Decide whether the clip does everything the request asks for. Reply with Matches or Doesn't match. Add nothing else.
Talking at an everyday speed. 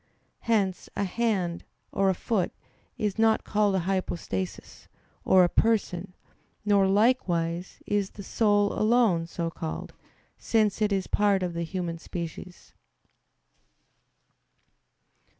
Doesn't match